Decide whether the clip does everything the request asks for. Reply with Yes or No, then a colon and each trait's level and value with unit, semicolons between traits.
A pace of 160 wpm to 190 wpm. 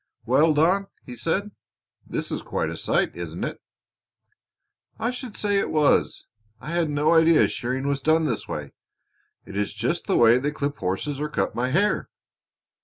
Yes: average, 175 wpm